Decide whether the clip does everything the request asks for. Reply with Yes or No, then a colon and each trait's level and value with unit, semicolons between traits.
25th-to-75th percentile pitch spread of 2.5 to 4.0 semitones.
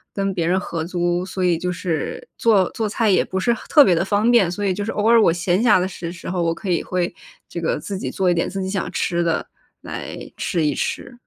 Yes: average, 2.8 semitones